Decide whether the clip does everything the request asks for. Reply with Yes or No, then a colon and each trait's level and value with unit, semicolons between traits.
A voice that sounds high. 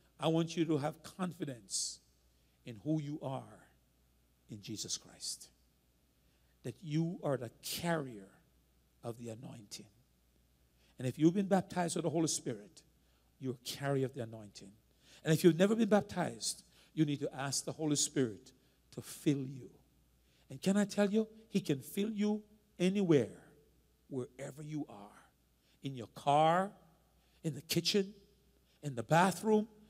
No: medium, 140 Hz